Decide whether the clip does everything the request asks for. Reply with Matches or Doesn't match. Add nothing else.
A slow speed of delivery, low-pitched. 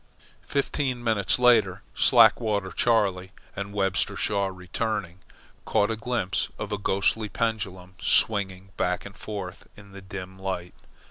Matches